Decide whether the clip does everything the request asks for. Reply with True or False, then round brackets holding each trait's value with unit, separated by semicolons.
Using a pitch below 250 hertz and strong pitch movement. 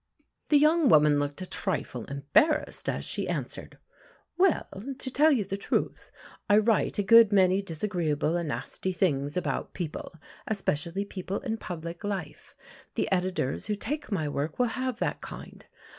True (190 Hz; 5.8 semitones)